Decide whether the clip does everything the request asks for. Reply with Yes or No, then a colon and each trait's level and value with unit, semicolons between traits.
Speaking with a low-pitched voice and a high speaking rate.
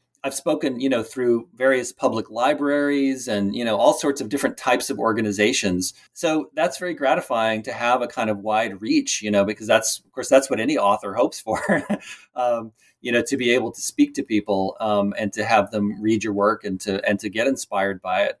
Yes: low, 110 Hz; fast, 220 wpm